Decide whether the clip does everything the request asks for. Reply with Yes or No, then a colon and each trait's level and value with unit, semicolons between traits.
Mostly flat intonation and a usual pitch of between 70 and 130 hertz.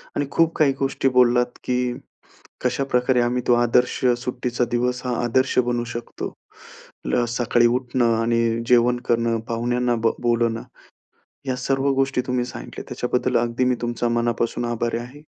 Yes: narrow, 1.1 semitones; low, 120 Hz